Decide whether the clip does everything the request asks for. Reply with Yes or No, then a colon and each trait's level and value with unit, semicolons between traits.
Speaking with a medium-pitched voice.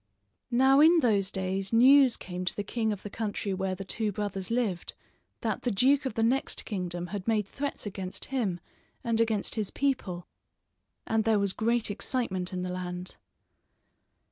No: high, 210 Hz